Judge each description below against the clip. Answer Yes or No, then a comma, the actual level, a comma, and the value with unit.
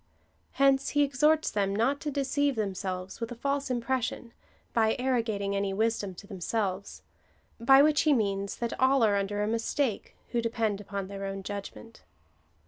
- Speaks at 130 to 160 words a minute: No, average, 170 wpm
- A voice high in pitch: Yes, high, 225 Hz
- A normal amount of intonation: Yes, average, 4.9 semitones